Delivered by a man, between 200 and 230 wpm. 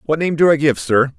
No: male; fast, 305 wpm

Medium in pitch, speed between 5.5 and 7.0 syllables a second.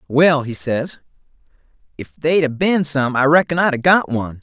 No: medium, 145 Hz; 4.9 syllables/s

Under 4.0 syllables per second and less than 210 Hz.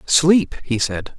Yes: 2.9 syllables/s; medium, 140 Hz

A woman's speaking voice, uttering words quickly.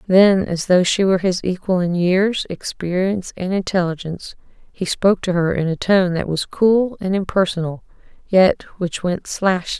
No: female; average, 170 wpm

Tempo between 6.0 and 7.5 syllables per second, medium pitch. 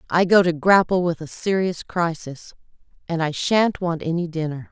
No: 4.8 syllables/s; medium, 170 Hz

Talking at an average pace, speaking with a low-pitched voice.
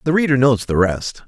No: fast, 235 wpm; low, 130 Hz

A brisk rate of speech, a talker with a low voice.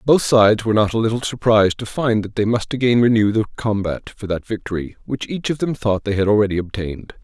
Yes: fast, 230 wpm; low, 110 Hz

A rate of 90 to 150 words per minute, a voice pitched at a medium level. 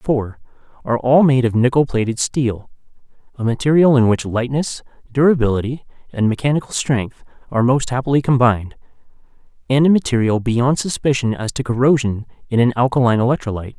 No: average, 140 wpm; low, 125 Hz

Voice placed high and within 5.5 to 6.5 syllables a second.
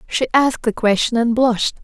Yes: high, 235 Hz; 5.8 syllables/s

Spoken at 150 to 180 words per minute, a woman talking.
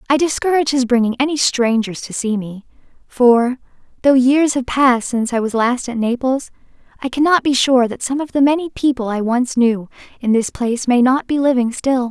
No: fast, 205 wpm; female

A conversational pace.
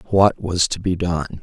No: fast, 210 wpm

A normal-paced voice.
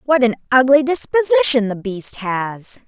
Yes: average, 145 wpm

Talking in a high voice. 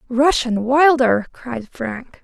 Yes: very high, 255 Hz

